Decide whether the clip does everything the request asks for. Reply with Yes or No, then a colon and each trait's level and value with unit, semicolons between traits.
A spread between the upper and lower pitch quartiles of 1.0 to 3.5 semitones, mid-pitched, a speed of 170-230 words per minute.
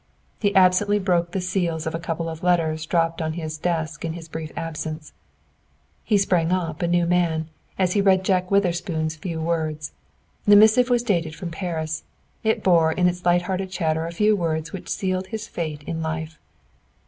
Yes: narrow, 2.6 semitones; medium, 170 Hz; average, 185 wpm